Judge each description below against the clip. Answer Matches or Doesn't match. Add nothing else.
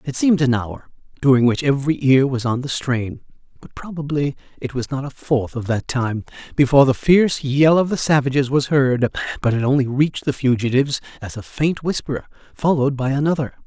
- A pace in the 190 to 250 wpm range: Matches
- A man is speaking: Matches